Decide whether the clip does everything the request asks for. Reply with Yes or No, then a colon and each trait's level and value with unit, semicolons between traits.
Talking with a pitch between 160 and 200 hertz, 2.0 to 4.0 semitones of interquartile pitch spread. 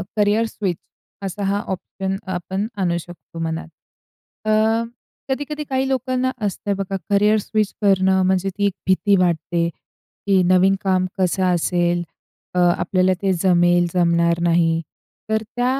Yes: high, 190 Hz; average, 2.8 semitones